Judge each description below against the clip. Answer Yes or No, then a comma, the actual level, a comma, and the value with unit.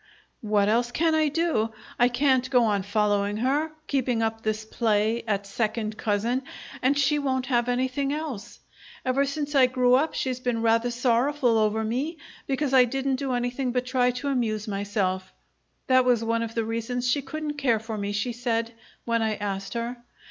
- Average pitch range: Yes, average, 3.2 semitones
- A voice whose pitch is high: Yes, high, 245 Hz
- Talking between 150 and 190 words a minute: Yes, average, 185 wpm